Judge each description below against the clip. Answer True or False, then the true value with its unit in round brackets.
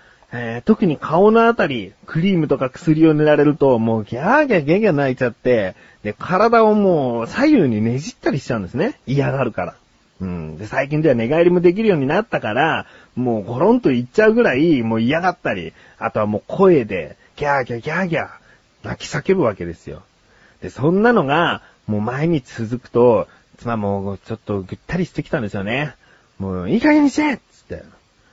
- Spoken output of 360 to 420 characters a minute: True (390 characters per minute)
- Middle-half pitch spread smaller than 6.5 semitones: False (7.9 semitones)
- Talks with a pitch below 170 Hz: True (135 Hz)